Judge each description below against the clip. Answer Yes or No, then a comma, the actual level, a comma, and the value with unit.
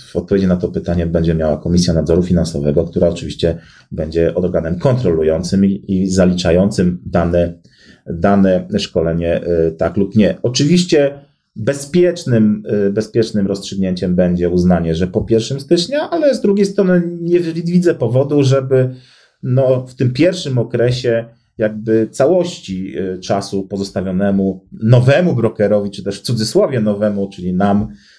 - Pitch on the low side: Yes, low, 105 Hz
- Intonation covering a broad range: Yes, wide, 6.2 semitones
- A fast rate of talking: No, average, 130 wpm